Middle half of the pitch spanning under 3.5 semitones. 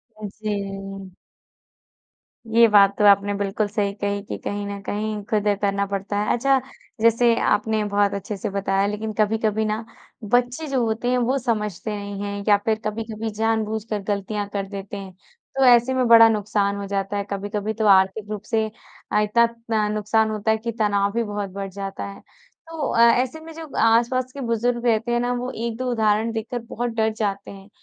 Yes: narrow, 2.4 semitones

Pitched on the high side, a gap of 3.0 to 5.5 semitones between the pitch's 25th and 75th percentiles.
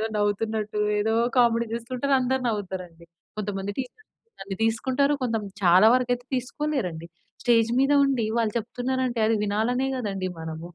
Yes: high, 230 Hz; average, 3.7 semitones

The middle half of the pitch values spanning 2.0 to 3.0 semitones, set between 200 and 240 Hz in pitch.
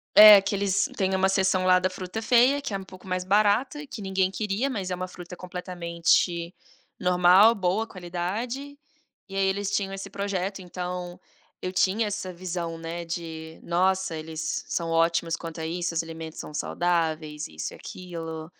No: narrow, 2.5 semitones; medium, 185 Hz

